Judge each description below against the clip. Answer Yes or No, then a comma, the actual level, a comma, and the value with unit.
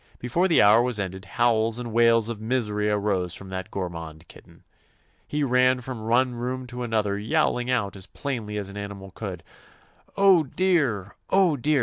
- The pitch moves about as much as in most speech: Yes, average, 4.1 semitones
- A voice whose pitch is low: Yes, low, 115 Hz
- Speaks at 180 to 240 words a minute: Yes, average, 190 wpm